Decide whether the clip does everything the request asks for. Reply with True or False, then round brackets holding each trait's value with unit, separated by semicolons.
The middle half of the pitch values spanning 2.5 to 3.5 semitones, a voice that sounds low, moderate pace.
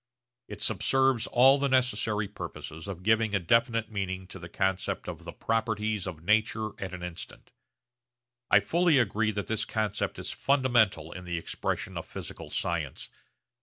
False (4.0 semitones; 105 Hz; 160 wpm)